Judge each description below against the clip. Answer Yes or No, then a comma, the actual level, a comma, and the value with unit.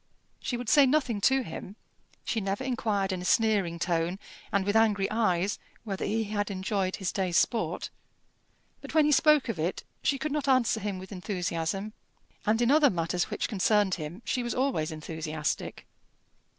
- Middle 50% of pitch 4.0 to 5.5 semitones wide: Yes, average, 4.7 semitones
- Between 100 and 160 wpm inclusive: No, average, 175 wpm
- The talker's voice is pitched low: No, high, 205 Hz